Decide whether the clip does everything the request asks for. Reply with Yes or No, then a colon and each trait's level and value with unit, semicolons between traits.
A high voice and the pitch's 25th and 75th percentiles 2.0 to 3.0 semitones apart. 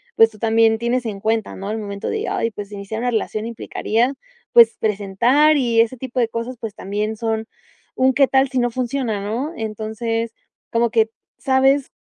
Yes: high, 230 Hz; narrow, 2.6 semitones